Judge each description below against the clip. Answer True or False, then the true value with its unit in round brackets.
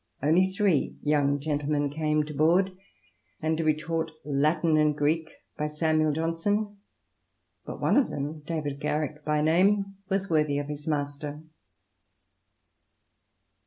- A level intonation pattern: True (1.9 semitones)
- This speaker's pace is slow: True (130 wpm)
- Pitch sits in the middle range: True (155 Hz)